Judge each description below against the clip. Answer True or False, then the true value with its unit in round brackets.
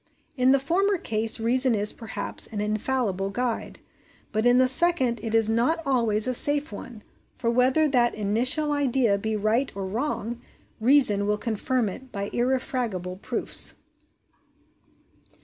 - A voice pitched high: True (235 Hz)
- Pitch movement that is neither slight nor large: True (3.5 semitones)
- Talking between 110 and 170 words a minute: True (145 wpm)